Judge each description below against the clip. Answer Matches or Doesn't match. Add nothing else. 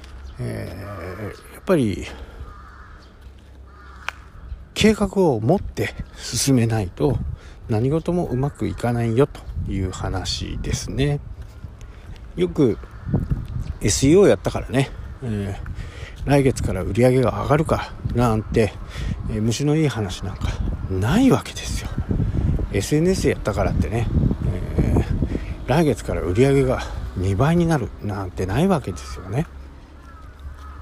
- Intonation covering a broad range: Matches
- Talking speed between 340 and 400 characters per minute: Doesn't match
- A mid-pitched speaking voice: Doesn't match